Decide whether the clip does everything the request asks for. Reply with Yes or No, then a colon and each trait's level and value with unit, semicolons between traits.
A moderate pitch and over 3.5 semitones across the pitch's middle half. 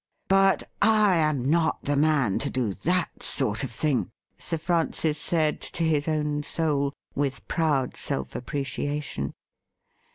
No: medium, 150 Hz; average, 3.1 semitones